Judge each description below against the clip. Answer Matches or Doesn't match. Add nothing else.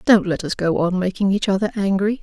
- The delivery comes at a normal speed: Doesn't match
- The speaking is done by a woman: Matches